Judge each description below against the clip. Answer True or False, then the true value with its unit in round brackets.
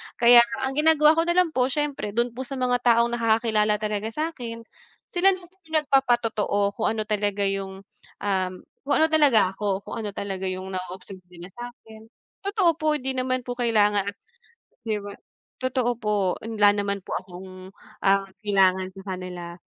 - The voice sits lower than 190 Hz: False (220 Hz)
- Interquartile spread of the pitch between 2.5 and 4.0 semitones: False (4.6 semitones)